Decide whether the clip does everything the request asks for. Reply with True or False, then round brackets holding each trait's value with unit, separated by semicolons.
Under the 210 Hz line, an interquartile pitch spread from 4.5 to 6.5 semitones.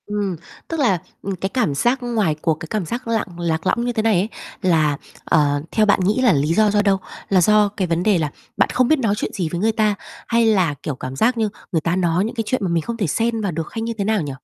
True (200 Hz; 5.1 semitones)